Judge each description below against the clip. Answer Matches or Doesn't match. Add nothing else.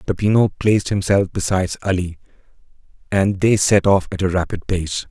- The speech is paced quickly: Doesn't match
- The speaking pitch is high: Doesn't match